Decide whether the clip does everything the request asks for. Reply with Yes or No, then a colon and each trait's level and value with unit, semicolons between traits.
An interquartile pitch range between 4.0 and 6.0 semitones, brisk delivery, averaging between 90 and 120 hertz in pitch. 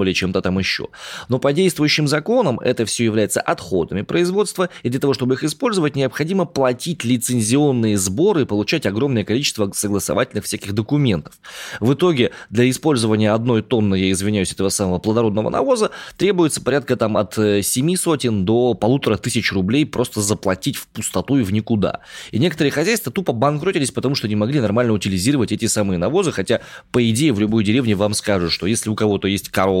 Yes: average, 5.0 semitones; fast, 175 wpm; low, 115 Hz